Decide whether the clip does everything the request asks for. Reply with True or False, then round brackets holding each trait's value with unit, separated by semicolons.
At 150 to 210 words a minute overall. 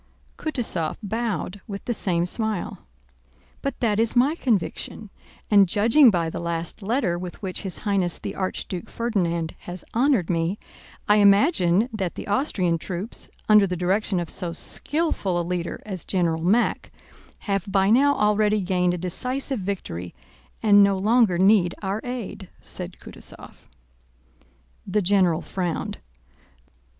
False (140 wpm)